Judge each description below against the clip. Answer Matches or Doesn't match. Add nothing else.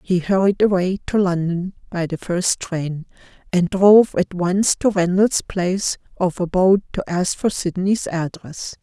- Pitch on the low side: Doesn't match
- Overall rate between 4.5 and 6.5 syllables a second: Doesn't match